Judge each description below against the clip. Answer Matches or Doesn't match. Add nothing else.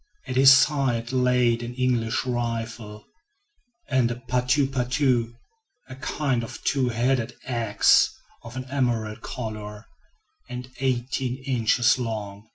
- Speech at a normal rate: Doesn't match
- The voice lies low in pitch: Matches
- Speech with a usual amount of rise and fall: Doesn't match